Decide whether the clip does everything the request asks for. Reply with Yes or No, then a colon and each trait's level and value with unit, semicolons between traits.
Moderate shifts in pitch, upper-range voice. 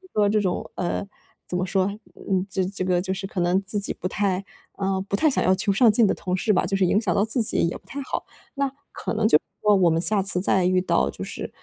No: narrow, 2.3 semitones; high, 195 Hz